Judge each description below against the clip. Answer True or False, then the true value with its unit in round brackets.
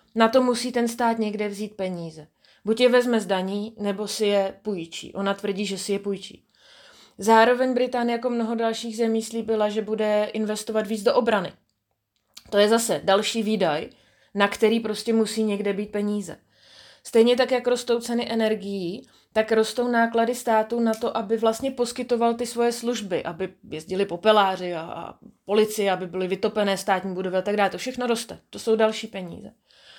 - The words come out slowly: False (170 wpm)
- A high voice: True (220 Hz)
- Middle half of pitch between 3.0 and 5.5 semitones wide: False (2.6 semitones)